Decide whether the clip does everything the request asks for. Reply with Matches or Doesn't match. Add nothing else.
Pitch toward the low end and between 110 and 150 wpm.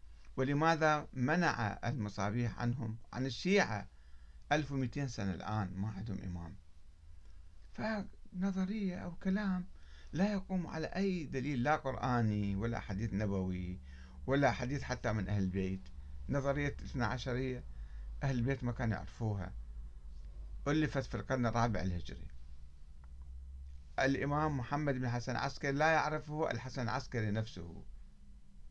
Matches